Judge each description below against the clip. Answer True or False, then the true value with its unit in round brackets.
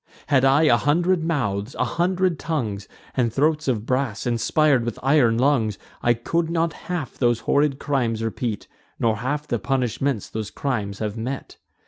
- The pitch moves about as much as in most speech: True (4.8 semitones)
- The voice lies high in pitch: False (130 Hz)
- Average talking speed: True (160 wpm)